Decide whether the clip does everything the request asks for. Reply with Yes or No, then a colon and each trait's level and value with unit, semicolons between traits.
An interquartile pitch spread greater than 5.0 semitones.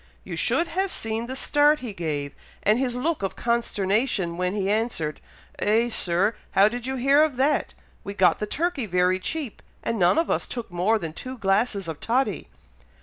Yes: wide, 5.5 semitones